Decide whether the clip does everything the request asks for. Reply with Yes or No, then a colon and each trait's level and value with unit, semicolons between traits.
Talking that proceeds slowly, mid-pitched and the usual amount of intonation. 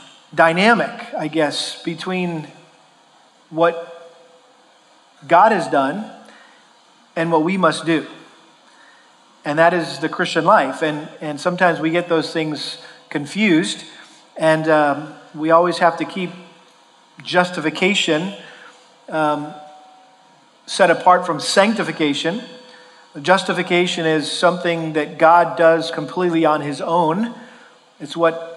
No: slow, 110 wpm; medium, 165 Hz; narrow, 2.3 semitones